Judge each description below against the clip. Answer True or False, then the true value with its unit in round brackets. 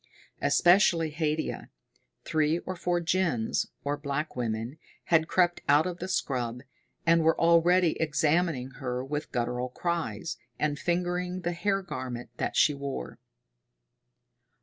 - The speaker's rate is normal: False (125 wpm)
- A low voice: False (160 Hz)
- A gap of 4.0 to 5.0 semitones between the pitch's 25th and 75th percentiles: True (4.4 semitones)